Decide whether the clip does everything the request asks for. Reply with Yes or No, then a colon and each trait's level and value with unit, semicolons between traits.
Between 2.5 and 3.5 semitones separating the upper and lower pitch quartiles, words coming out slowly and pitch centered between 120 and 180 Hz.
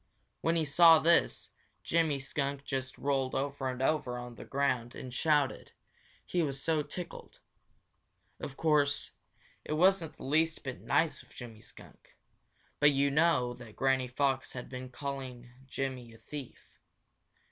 No: average, 3.0 semitones; average, 145 wpm; medium, 140 Hz